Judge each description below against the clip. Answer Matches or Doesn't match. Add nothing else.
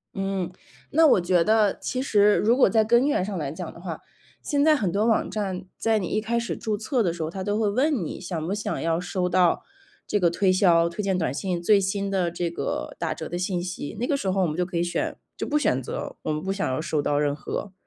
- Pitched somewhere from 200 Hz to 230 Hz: Doesn't match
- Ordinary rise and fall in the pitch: Matches